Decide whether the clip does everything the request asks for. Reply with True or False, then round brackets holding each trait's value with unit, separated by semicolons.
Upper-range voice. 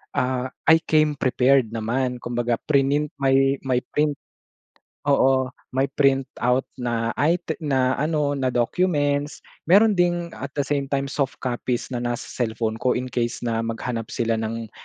False (130 Hz)